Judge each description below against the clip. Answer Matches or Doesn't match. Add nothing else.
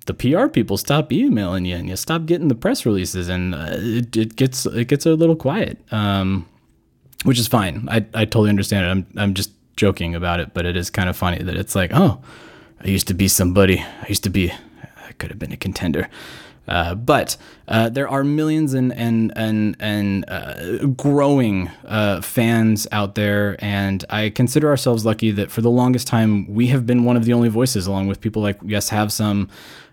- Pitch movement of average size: Matches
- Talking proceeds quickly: Matches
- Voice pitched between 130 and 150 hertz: Doesn't match